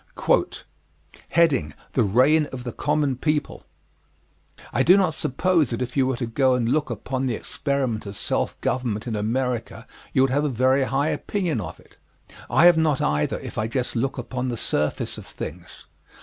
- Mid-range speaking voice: No, low, 130 Hz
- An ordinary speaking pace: Yes, average, 180 wpm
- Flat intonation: No, average, 3.9 semitones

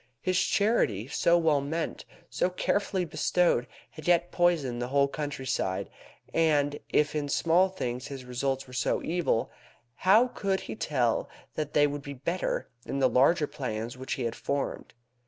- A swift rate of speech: No, average, 160 wpm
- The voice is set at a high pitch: No, medium, 145 Hz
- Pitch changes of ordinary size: Yes, average, 4.9 semitones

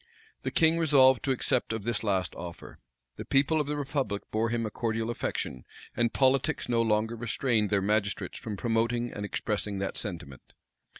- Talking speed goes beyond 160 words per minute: Yes, average, 175 wpm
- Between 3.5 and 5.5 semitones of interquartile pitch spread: Yes, average, 4.0 semitones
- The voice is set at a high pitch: No, low, 115 Hz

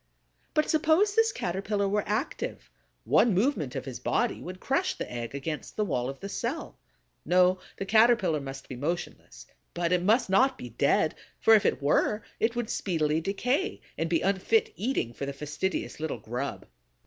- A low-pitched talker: No, medium, 185 Hz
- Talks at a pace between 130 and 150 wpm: No, average, 175 wpm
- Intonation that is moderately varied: No, wide, 8.0 semitones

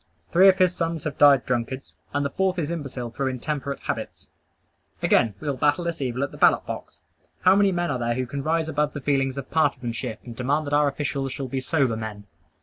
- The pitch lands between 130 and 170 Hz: Yes, medium, 140 Hz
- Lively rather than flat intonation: No, average, 3.6 semitones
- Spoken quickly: Yes, fast, 225 wpm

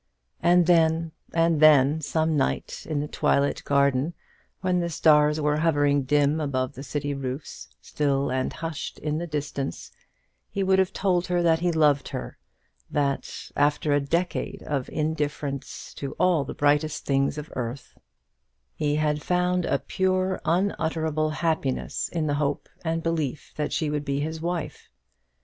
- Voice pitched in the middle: Yes, medium, 150 Hz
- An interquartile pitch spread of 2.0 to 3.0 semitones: Yes, narrow, 2.6 semitones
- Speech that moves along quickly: No, average, 155 wpm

